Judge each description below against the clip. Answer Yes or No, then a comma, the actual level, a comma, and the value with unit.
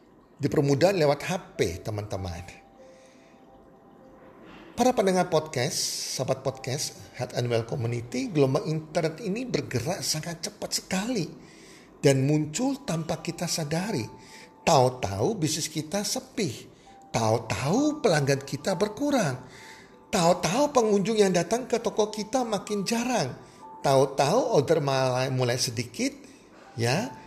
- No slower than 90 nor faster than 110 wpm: Yes, average, 105 wpm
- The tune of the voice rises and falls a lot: Yes, wide, 7.7 semitones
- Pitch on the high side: No, medium, 160 Hz